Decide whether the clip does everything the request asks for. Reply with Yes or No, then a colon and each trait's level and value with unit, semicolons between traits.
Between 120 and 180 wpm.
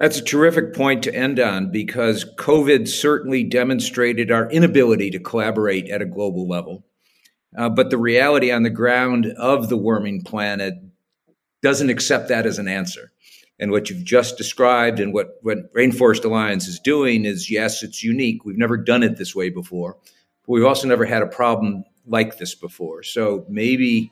Yes: average, 175 wpm